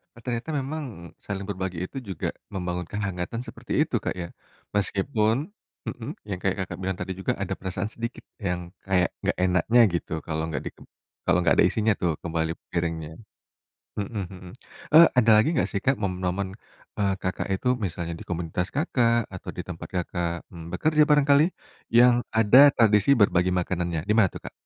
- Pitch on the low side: Yes, very low, 95 Hz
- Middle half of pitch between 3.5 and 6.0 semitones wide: Yes, average, 4.2 semitones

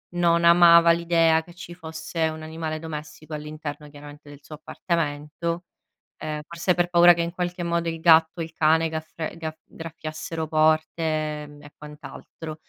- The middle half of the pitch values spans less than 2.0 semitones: Yes, narrow, 1.5 semitones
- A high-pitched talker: No, medium, 160 Hz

